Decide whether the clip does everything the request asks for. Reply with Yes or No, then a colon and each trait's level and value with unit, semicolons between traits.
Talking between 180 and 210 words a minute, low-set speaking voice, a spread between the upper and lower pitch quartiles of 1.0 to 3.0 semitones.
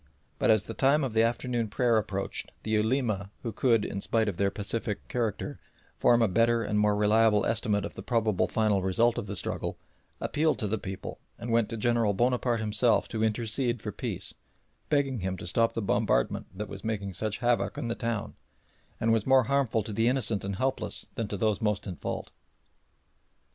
Yes: average, 195 wpm; low, 110 Hz; narrow, 2.4 semitones